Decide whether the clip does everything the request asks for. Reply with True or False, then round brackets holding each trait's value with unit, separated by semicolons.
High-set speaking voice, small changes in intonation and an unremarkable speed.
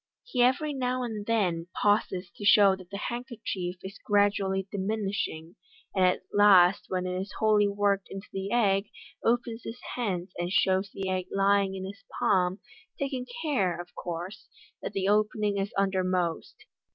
True (195 Hz; 2.3 semitones; 165 wpm)